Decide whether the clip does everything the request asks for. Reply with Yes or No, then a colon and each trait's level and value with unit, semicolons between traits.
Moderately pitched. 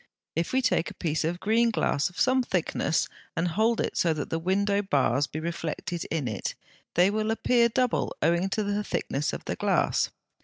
Yes: medium, 180 Hz